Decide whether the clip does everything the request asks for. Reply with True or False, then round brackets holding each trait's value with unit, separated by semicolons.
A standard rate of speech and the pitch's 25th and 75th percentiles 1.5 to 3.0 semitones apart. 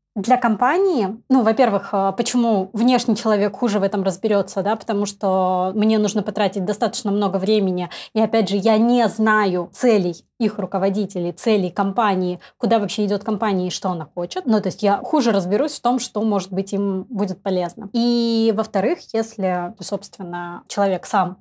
False (165 wpm; 2.7 semitones)